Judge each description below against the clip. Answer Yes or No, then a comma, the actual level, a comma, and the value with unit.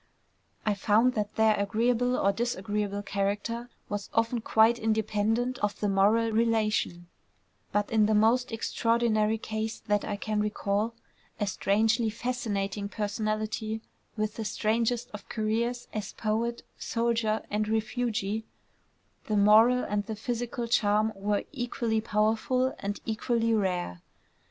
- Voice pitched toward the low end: No, high, 220 Hz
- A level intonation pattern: Yes, narrow, 1.8 semitones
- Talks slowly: Yes, slow, 125 wpm